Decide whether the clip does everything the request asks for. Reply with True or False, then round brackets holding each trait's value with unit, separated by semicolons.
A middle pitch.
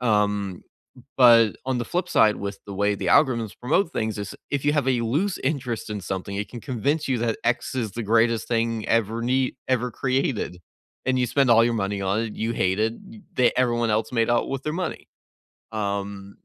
False (115 Hz)